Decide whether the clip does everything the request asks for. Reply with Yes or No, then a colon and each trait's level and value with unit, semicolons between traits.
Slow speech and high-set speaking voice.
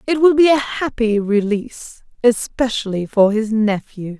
Yes: slow, 130 wpm; high, 230 Hz